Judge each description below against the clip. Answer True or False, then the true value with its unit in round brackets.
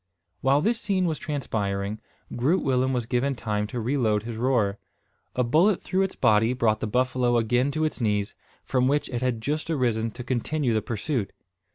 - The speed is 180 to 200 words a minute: True (185 wpm)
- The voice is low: True (125 Hz)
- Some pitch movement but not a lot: True (4.1 semitones)